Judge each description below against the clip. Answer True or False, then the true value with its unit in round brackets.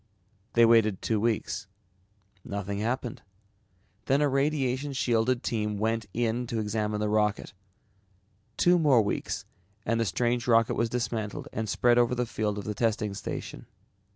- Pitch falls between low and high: False (115 Hz)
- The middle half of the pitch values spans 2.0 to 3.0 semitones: True (2.5 semitones)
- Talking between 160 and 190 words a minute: False (150 wpm)